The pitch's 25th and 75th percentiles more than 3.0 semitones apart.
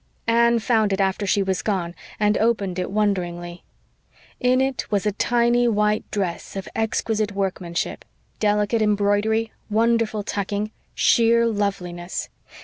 No: average, 2.7 semitones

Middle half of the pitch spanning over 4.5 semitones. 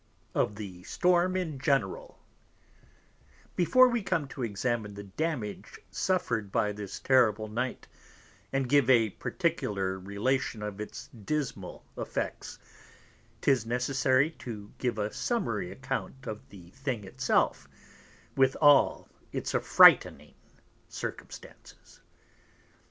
Yes: wide, 5.6 semitones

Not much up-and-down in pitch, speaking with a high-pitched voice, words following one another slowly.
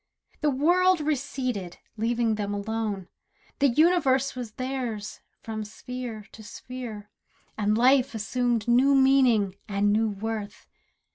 No: average, 3.9 semitones; high, 235 Hz; slow, 120 wpm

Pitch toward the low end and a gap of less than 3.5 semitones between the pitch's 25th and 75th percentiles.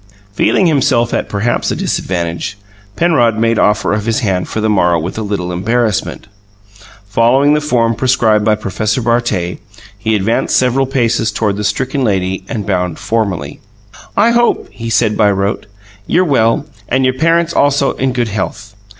No: low, 110 Hz; average, 4.1 semitones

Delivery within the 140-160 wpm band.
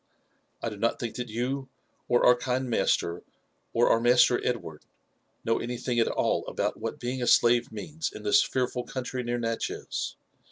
No: average, 170 wpm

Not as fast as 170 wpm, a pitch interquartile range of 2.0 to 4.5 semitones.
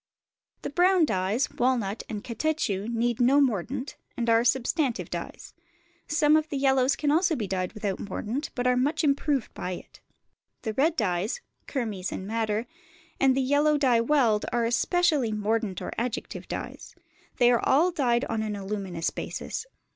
No: average, 160 wpm; average, 5.0 semitones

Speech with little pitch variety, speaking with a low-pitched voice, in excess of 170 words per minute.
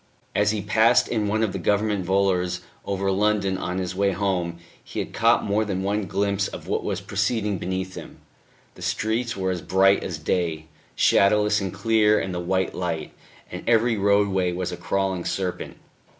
Yes: narrow, 2.1 semitones; low, 100 Hz; average, 180 wpm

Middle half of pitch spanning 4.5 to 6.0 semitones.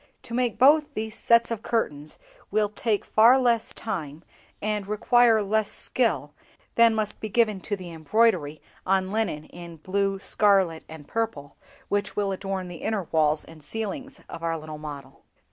Yes: average, 5.2 semitones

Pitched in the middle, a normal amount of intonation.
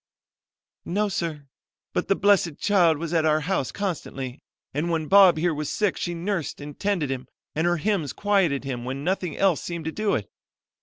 Yes: medium, 170 Hz; average, 4.7 semitones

